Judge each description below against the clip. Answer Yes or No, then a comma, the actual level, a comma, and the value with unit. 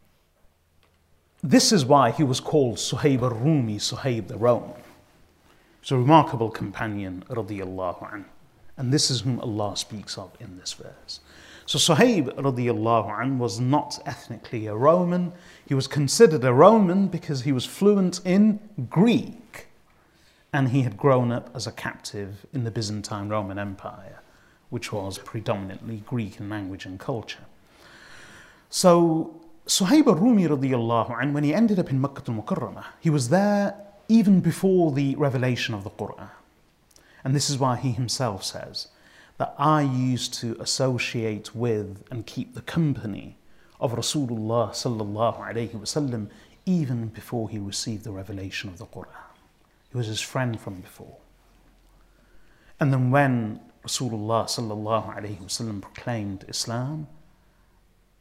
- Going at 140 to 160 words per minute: Yes, average, 145 wpm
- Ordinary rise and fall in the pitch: No, wide, 5.7 semitones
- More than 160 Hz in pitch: No, low, 120 Hz